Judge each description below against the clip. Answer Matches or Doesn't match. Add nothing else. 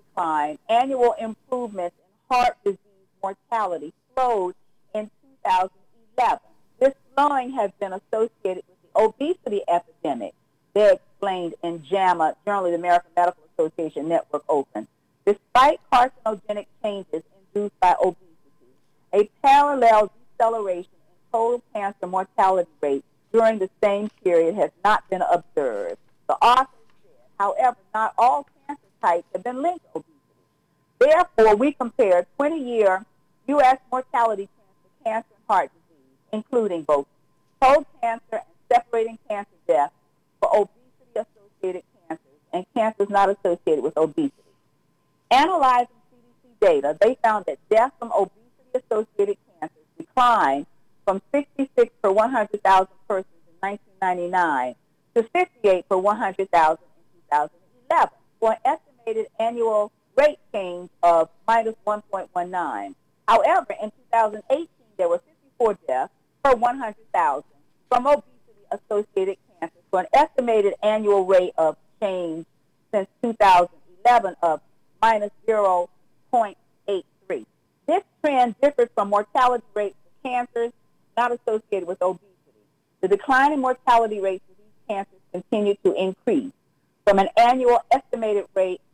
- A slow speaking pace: Matches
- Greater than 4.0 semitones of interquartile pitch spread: Matches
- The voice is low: Doesn't match